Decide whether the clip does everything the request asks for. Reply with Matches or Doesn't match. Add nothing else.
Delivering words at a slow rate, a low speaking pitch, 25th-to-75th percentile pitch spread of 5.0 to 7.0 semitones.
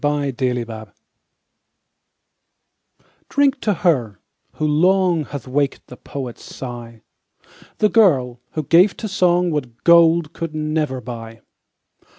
Doesn't match